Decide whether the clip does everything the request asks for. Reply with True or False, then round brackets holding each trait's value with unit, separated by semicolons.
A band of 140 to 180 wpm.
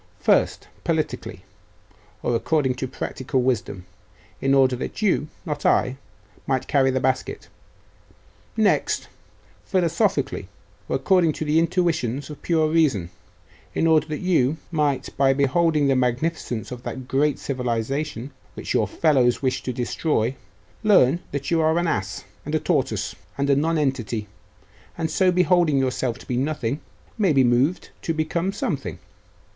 True (145 wpm)